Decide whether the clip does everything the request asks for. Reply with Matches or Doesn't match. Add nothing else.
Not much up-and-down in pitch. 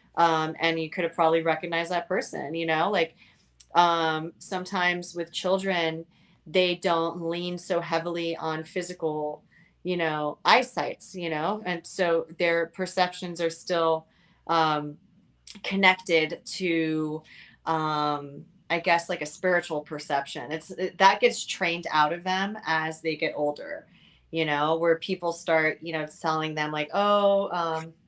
Matches